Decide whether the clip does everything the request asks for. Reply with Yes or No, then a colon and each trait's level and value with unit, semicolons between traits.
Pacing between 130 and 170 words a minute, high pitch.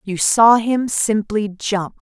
Yes: average, 140 wpm; high, 215 Hz